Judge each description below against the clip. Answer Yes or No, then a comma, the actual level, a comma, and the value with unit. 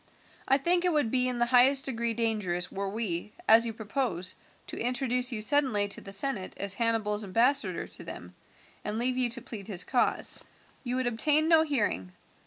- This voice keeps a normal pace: Yes, average, 190 wpm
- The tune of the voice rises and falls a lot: No, average, 3.8 semitones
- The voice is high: Yes, high, 235 Hz